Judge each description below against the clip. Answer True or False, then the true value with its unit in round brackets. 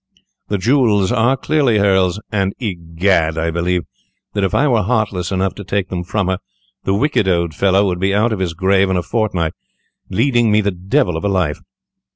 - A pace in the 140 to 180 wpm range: False (195 wpm)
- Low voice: True (95 Hz)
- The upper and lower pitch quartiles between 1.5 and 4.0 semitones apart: True (3.0 semitones)